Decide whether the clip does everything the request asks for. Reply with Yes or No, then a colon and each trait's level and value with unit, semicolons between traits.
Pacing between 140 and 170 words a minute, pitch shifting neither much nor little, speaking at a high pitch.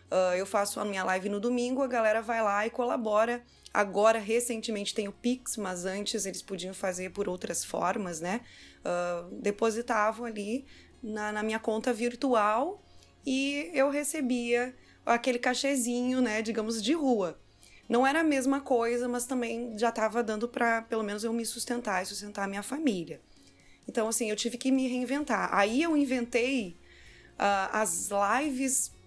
Yes: average, 160 wpm; average, 3.5 semitones; high, 225 Hz